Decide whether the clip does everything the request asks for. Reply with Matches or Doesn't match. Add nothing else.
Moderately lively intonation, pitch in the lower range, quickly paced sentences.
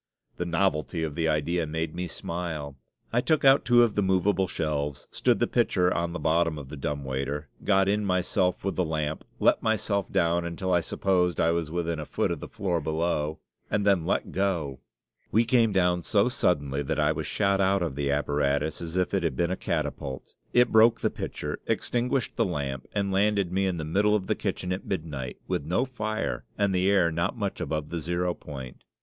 Matches